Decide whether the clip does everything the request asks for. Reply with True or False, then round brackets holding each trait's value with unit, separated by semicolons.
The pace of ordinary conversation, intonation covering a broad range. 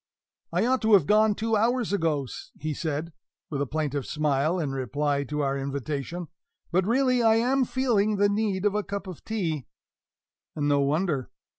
True (175 wpm; 7.0 semitones)